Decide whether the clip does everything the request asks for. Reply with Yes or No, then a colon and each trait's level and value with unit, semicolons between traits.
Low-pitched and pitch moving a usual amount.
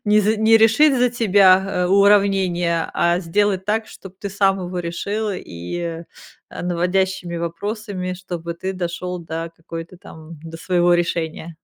No: medium, 180 Hz; average, 3.0 semitones